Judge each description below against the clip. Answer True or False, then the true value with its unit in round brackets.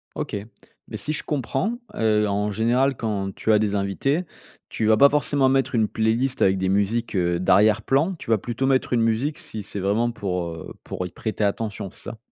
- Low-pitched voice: True (110 Hz)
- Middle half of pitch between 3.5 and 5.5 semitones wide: True (4.7 semitones)